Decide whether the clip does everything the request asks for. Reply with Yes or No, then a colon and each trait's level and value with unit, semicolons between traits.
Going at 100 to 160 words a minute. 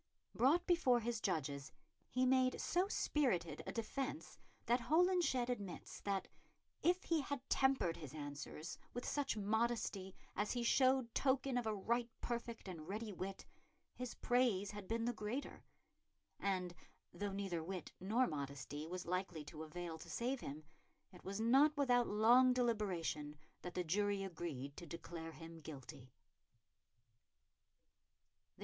Yes: average, 140 wpm